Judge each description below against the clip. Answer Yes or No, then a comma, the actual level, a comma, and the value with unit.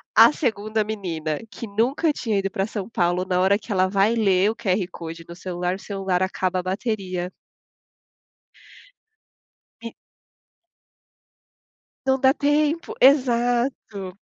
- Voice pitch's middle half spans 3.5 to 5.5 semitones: Yes, average, 4.2 semitones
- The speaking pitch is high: Yes, high, 200 Hz